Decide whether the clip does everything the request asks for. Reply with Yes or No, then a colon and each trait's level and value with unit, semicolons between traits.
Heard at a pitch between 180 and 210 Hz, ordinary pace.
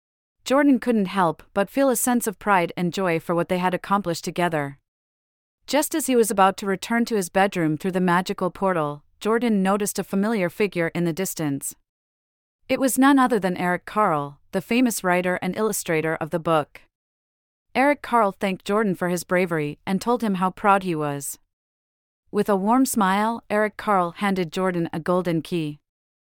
Yes: medium, 185 Hz; average, 180 wpm